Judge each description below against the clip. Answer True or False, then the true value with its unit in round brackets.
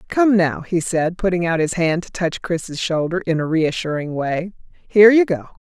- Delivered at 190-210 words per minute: True (205 wpm)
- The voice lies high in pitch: False (175 Hz)